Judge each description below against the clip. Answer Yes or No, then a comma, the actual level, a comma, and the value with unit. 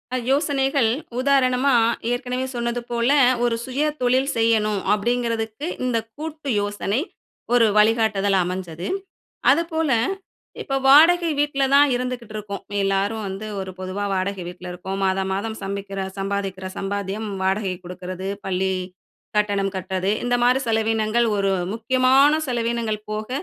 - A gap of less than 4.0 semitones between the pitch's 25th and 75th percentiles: No, average, 4.5 semitones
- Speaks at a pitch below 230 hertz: Yes, high, 220 Hz